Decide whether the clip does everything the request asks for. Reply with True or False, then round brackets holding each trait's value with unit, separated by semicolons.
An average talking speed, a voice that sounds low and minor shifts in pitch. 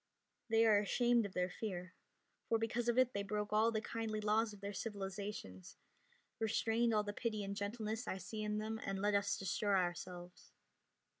False (180 wpm; 210 Hz; 2.2 semitones)